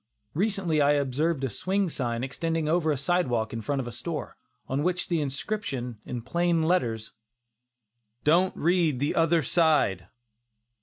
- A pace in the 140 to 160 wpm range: Yes, average, 155 wpm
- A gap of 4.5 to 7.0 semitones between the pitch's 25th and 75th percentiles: Yes, average, 5.1 semitones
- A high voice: No, medium, 155 Hz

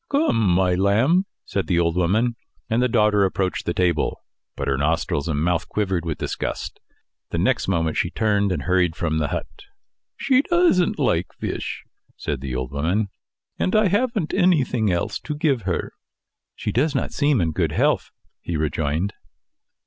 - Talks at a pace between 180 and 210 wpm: No, average, 170 wpm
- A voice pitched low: Yes, very low, 95 Hz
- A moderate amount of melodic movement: No, wide, 7.6 semitones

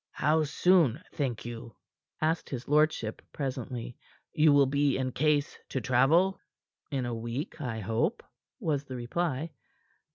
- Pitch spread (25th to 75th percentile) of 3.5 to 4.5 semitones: Yes, average, 4.1 semitones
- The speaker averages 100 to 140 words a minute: Yes, slow, 135 wpm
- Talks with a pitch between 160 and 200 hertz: No, medium, 140 Hz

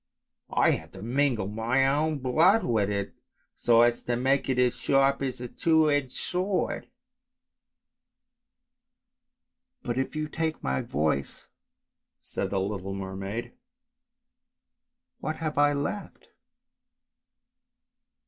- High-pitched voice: No, low, 130 Hz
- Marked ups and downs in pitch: Yes, wide, 5.7 semitones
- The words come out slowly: Yes, slow, 120 wpm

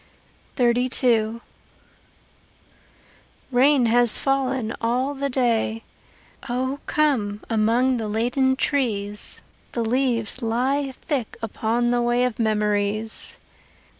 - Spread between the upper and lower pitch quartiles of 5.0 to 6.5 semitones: No, average, 2.8 semitones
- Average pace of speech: No, slow, 95 wpm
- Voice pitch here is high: Yes, high, 240 Hz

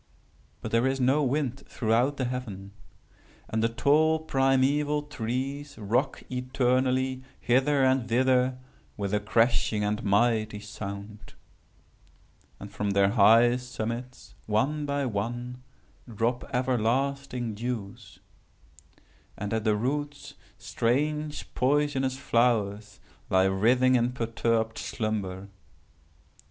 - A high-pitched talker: No, low, 125 Hz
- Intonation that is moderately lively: Yes, average, 3.5 semitones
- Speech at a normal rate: No, slow, 105 wpm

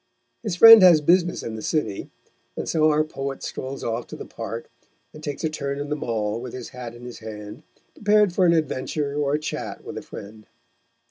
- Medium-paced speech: No, fast, 210 wpm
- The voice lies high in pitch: No, medium, 140 Hz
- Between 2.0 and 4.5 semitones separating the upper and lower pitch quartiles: No, average, 5.1 semitones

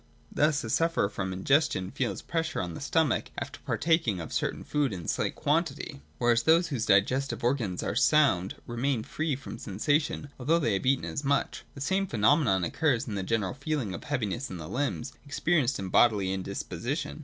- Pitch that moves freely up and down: Yes, wide, 6.9 semitones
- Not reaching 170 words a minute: No, average, 185 wpm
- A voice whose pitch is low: Yes, low, 130 Hz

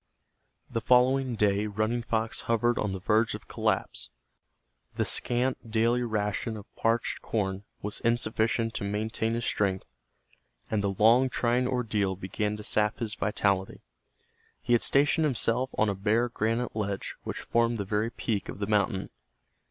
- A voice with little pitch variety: Yes, narrow, 2.3 semitones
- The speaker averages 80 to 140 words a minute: No, average, 155 wpm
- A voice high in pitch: No, low, 110 Hz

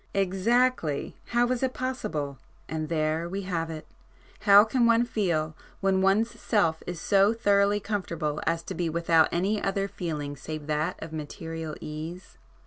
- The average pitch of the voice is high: No, medium, 180 Hz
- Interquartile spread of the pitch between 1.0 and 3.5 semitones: No, average, 4.6 semitones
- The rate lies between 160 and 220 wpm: No, average, 145 wpm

